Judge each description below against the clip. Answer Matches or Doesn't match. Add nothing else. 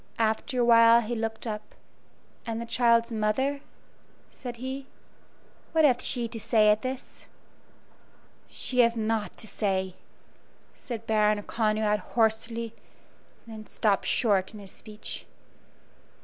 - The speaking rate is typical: Doesn't match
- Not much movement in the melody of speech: Matches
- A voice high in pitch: Matches